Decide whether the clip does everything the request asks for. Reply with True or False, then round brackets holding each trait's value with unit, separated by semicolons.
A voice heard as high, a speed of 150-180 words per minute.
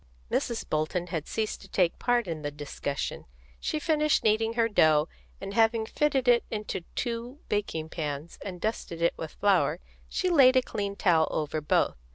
True (200 Hz; 175 wpm)